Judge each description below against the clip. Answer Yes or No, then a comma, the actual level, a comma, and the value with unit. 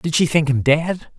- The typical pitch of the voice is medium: Yes, medium, 155 Hz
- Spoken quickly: Yes, fast, 255 wpm